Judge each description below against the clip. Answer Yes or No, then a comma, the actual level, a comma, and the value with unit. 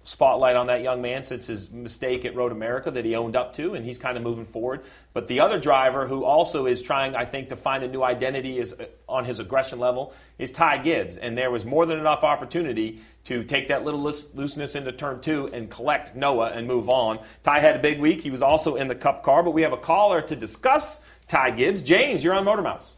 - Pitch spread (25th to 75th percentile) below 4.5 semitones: Yes, average, 3.4 semitones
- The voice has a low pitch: Yes, low, 130 Hz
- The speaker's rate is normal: No, fast, 245 wpm